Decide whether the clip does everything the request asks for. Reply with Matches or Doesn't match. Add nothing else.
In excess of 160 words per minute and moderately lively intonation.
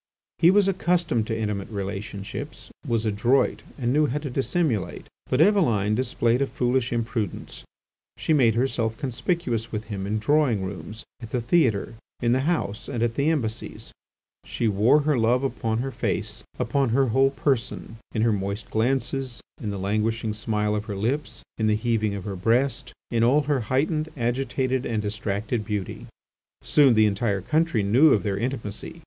Matches